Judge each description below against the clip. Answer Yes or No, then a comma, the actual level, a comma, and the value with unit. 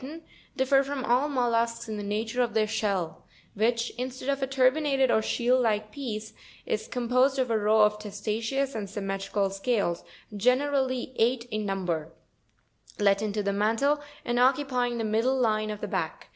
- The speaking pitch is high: Yes, high, 230 Hz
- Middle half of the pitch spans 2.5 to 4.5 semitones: Yes, average, 3.6 semitones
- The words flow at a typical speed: Yes, average, 175 wpm